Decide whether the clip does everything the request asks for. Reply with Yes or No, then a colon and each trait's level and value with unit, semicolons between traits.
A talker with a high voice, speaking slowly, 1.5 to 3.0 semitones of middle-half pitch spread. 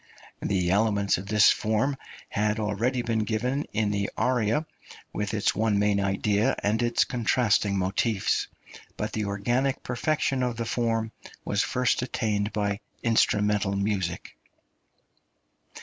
No: low, 105 Hz; slow, 130 wpm; average, 2.7 semitones